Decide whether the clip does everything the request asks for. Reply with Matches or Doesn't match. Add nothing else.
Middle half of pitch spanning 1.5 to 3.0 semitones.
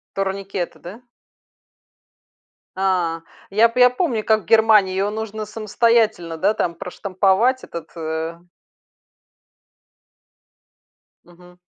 Doesn't match